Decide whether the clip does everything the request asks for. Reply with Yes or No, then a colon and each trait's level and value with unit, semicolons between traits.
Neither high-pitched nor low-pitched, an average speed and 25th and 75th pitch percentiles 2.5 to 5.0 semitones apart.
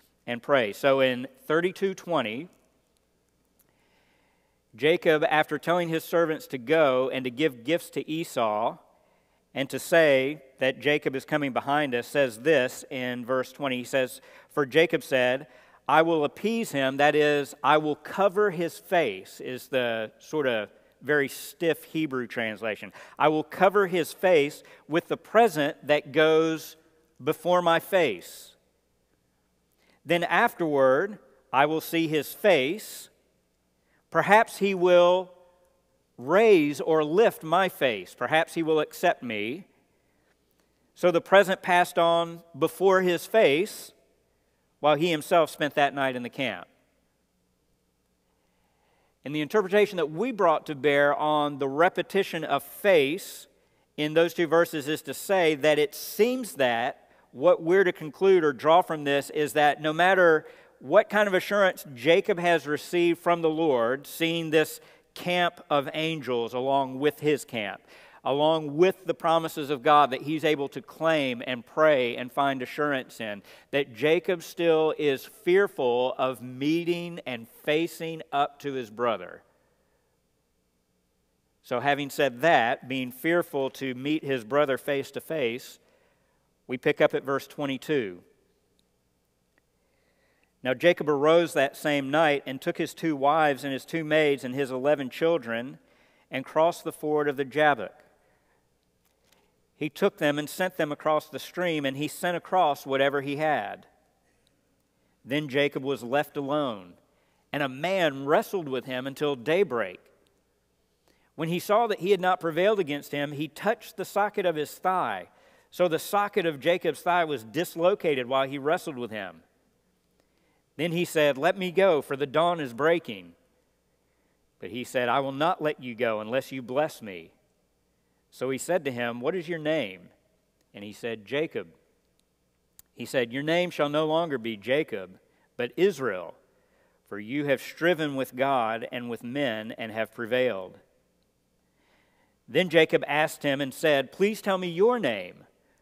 Yes: medium, 150 Hz; average, 150 wpm; average, 4.4 semitones